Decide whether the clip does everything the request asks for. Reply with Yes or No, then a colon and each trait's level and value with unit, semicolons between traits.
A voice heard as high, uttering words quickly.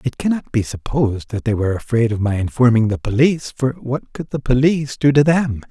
No: low, 125 Hz; fast, 220 wpm